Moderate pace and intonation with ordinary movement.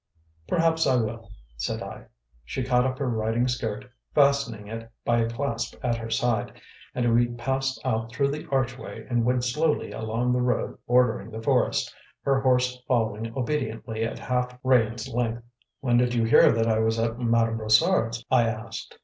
No: average, 175 wpm; narrow, 2.1 semitones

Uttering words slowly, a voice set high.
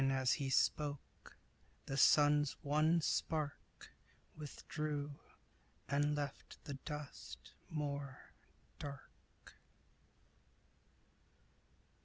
No: slow, 75 wpm; medium, 145 Hz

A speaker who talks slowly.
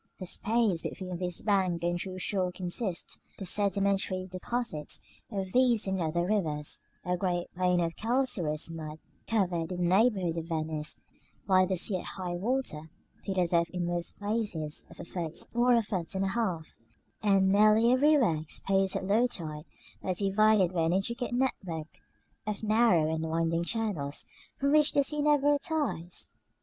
No: average, 170 wpm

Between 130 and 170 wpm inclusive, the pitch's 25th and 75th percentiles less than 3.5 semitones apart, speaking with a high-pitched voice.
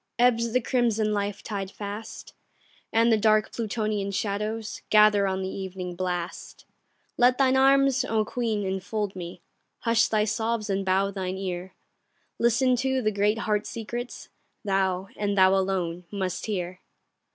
Yes: average, 145 wpm; average, 3.0 semitones; high, 210 Hz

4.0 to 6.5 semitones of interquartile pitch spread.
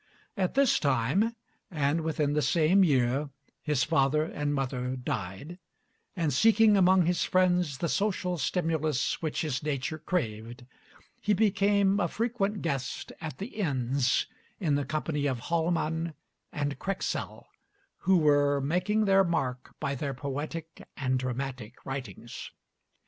Yes: average, 5.0 semitones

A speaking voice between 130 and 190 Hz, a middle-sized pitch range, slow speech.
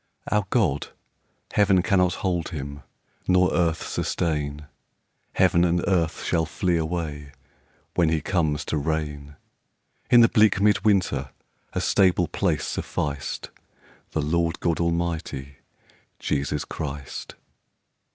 No: very low, 80 Hz; average, 3.6 semitones; slow, 115 wpm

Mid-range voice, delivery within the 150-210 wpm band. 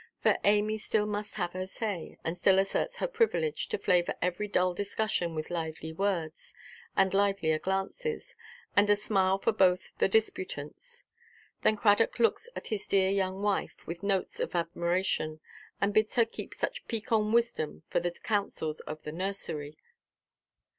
No: high, 195 Hz; average, 160 wpm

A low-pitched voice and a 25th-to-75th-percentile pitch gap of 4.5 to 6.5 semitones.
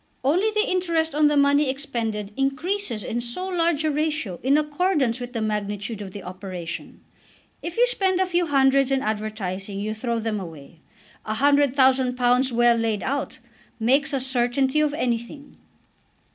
No: very high, 260 Hz; wide, 5.5 semitones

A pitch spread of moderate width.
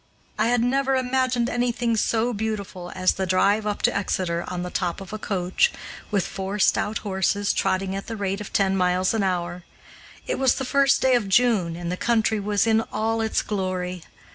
Yes: average, 3.7 semitones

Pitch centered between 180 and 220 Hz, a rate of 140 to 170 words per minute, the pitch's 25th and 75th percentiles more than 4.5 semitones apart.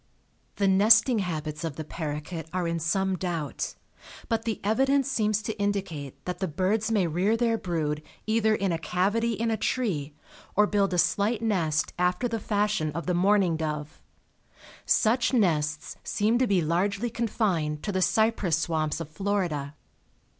Yes: high, 190 Hz; average, 160 wpm; average, 5.2 semitones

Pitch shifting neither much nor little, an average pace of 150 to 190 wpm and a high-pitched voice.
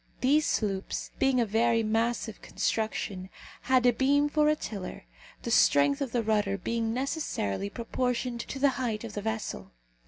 Yes: average, 3.5 semitones; average, 160 wpm; high, 230 Hz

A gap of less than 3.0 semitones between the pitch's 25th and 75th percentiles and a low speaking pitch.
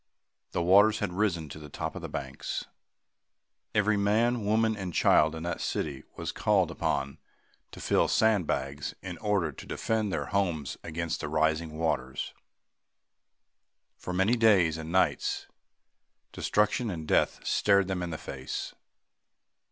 No: average, 4.8 semitones; very low, 90 Hz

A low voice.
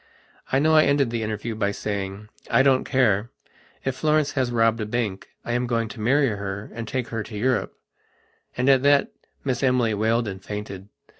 Yes: low, 115 Hz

